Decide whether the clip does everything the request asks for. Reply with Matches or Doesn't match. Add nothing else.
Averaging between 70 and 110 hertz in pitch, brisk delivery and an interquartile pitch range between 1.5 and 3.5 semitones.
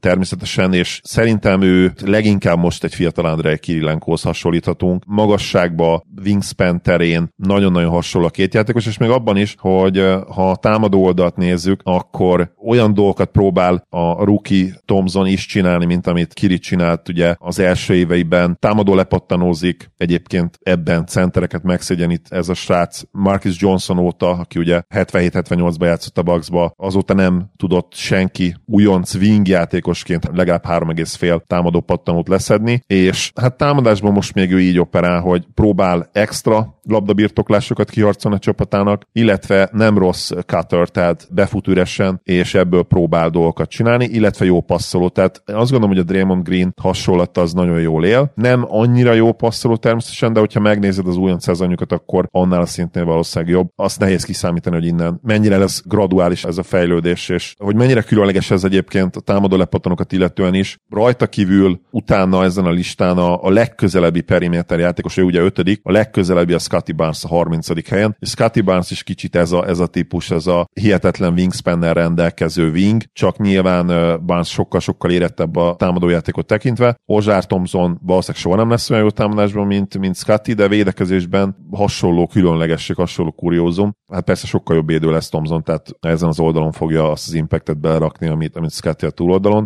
Matches